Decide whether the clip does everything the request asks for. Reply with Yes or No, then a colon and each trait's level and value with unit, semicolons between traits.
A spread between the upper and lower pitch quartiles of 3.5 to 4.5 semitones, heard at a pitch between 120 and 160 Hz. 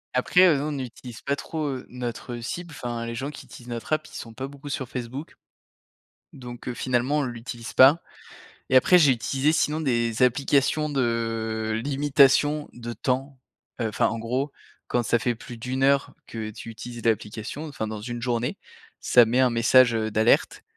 No: average, 3.0 semitones; low, 125 Hz